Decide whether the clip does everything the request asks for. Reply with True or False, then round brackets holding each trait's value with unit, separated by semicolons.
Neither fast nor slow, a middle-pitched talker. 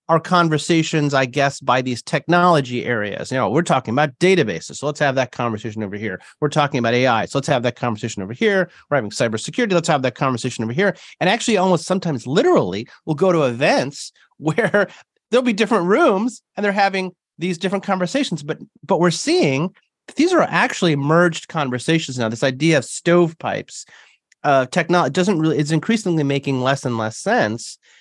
True (180 wpm; 160 Hz)